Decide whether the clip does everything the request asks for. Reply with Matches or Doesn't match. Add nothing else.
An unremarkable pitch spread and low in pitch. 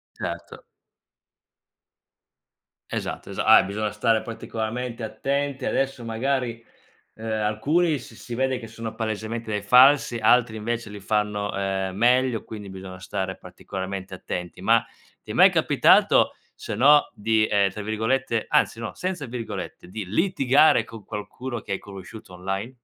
Matches